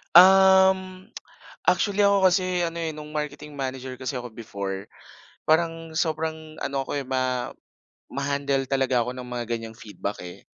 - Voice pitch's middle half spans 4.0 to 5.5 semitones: Yes, average, 5.0 semitones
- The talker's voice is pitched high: No, medium, 145 Hz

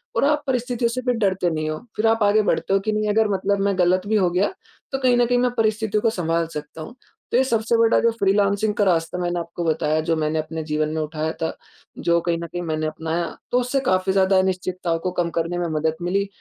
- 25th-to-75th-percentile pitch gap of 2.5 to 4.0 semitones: No, average, 4.7 semitones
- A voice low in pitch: No, high, 190 Hz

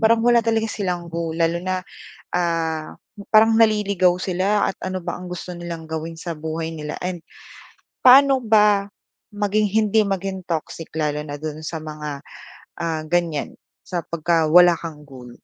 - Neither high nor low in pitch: Yes, medium, 175 Hz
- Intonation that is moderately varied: Yes, average, 4.1 semitones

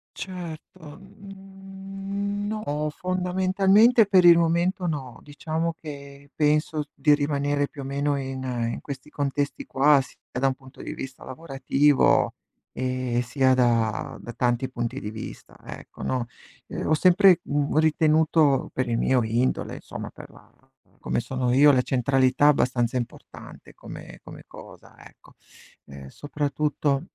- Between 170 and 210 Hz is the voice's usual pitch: No, medium, 145 Hz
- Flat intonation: No, average, 4.5 semitones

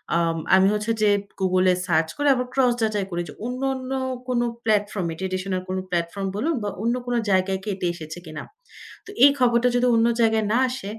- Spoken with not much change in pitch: No, average, 4.5 semitones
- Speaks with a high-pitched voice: Yes, high, 205 Hz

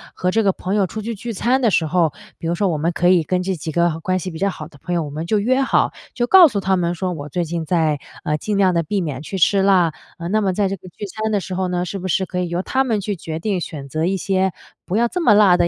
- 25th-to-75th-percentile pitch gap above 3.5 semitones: No, average, 3.2 semitones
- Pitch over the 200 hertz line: No, medium, 185 Hz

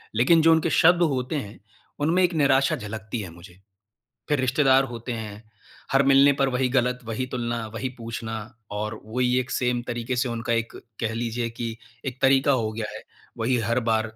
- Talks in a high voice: No, low, 120 Hz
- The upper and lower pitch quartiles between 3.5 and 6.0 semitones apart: No, average, 2.9 semitones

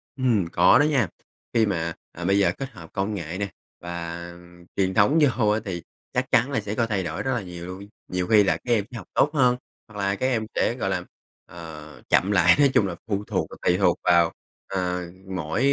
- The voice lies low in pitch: Yes, low, 100 Hz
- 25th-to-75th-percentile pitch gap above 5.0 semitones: No, average, 4.7 semitones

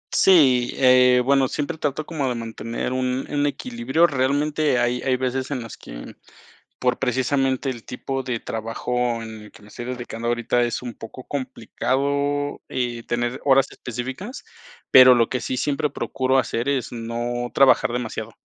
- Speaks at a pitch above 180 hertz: No, low, 130 Hz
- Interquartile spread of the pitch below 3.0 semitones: Yes, narrow, 2.4 semitones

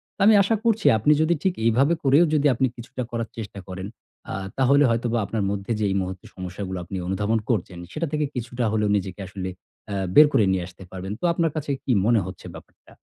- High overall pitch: No, low, 115 Hz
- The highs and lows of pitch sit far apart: Yes, wide, 6.6 semitones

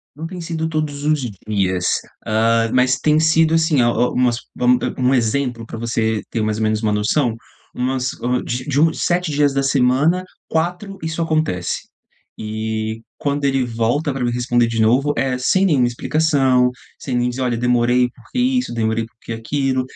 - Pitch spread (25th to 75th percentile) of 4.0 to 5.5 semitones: Yes, average, 4.6 semitones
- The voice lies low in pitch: Yes, low, 125 Hz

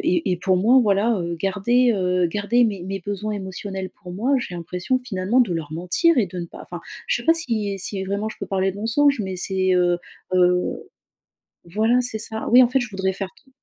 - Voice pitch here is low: No, high, 195 Hz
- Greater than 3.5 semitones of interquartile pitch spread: Yes, average, 4.1 semitones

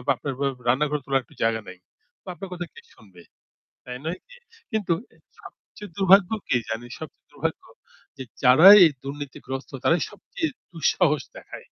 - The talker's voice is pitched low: No, medium, 150 Hz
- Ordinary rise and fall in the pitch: No, wide, 6.2 semitones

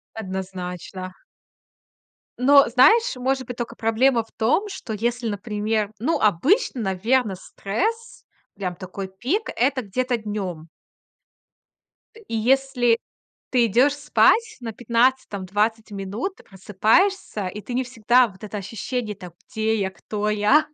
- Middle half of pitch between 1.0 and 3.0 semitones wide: No, average, 4.3 semitones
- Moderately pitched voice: No, high, 225 Hz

